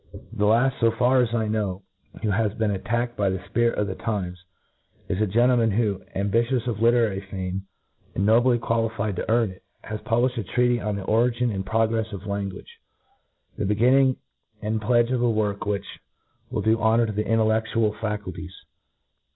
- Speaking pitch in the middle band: No, low, 110 Hz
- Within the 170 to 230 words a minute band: Yes, average, 185 wpm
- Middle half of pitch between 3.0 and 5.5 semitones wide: No, narrow, 2.6 semitones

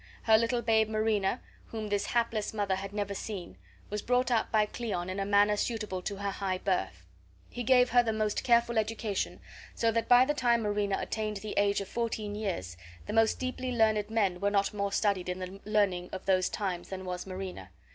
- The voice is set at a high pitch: Yes, high, 210 Hz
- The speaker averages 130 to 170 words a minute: No, fast, 205 wpm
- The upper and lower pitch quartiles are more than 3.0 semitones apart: No, average, 2.7 semitones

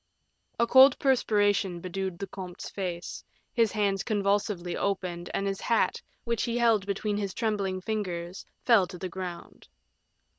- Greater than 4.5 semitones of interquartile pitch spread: No, average, 2.9 semitones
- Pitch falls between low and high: No, high, 195 Hz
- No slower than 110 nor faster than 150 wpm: Yes, average, 145 wpm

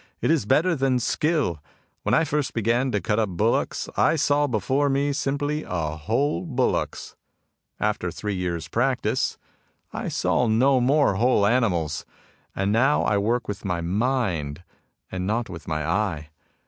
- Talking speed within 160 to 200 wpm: No, average, 150 wpm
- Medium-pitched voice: No, low, 115 Hz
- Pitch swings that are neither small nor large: No, wide, 6.8 semitones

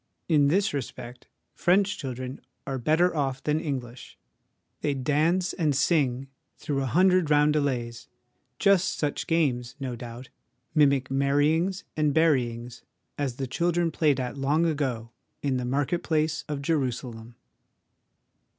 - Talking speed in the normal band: No, slow, 130 wpm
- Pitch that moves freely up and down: No, average, 3.8 semitones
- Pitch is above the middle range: No, medium, 140 Hz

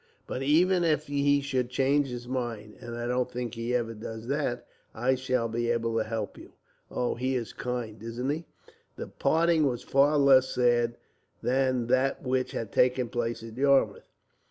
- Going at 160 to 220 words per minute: Yes, average, 180 wpm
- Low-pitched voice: Yes, low, 125 Hz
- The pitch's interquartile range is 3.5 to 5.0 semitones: No, narrow, 2.5 semitones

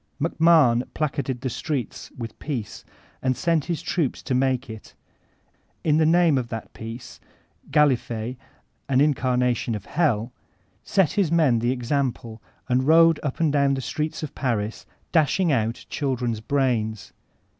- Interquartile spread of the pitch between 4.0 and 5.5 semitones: Yes, average, 4.4 semitones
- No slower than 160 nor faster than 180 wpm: No, average, 145 wpm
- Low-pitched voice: Yes, low, 130 Hz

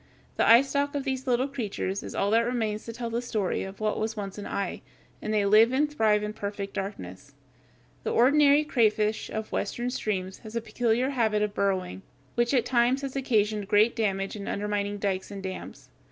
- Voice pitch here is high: Yes, high, 215 Hz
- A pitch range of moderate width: Yes, average, 3.3 semitones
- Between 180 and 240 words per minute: Yes, average, 195 wpm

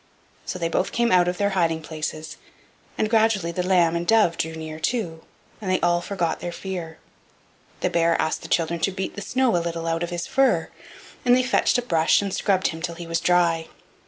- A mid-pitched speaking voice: Yes, medium, 175 Hz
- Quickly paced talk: Yes, fast, 215 wpm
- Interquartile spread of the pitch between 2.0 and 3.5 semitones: Yes, average, 2.9 semitones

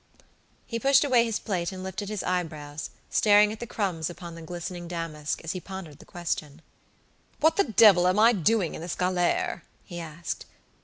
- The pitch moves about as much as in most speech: Yes, average, 4.0 semitones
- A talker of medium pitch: Yes, medium, 180 Hz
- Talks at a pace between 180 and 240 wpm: Yes, average, 185 wpm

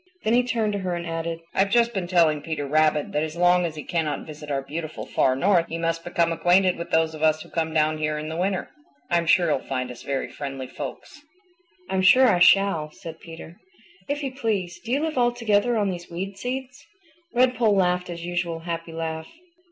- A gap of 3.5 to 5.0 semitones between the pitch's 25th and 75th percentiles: Yes, average, 3.9 semitones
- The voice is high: No, medium, 170 Hz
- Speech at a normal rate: No, fast, 215 wpm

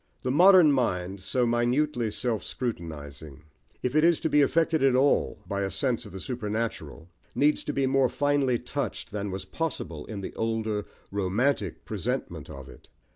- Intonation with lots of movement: Yes, wide, 6.1 semitones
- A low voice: Yes, low, 120 Hz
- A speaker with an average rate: Yes, average, 170 wpm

